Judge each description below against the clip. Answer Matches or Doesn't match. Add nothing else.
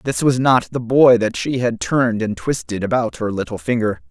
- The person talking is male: Matches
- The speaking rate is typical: Doesn't match